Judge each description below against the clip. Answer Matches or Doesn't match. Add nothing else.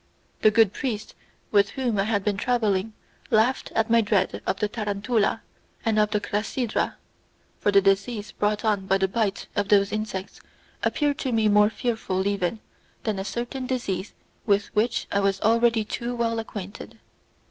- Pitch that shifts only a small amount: Matches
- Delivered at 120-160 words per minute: Doesn't match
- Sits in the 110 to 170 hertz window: Doesn't match